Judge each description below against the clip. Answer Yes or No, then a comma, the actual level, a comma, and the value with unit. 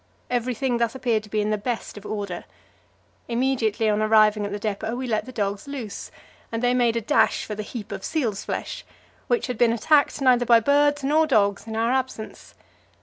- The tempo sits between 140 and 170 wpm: No, fast, 205 wpm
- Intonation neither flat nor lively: Yes, average, 3.2 semitones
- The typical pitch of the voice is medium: No, high, 230 Hz